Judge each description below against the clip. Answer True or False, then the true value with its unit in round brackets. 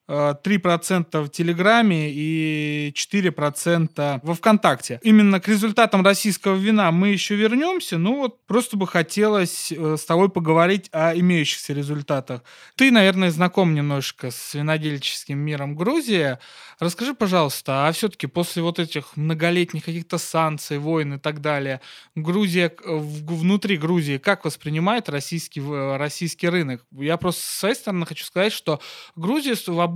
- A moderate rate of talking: True (130 wpm)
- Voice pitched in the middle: True (170 Hz)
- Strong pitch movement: False (4.7 semitones)